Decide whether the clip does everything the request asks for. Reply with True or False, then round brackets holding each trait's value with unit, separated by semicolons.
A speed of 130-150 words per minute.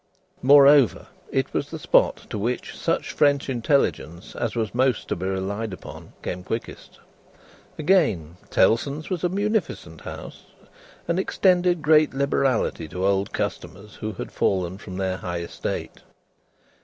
True (140 wpm)